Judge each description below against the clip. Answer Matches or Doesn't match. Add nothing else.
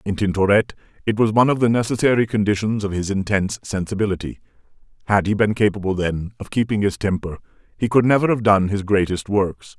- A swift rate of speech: Doesn't match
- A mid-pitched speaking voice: Doesn't match